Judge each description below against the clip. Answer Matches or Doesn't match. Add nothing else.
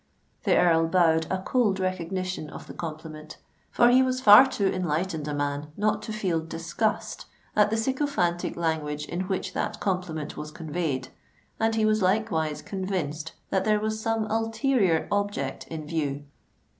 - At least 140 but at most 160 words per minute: Matches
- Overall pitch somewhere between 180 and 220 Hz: Matches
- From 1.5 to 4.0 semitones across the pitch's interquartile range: Doesn't match